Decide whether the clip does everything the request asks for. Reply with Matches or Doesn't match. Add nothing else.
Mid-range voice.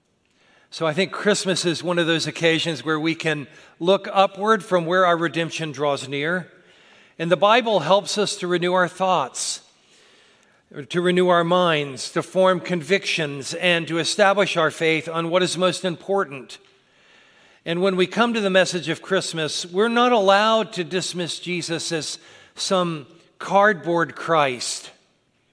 Matches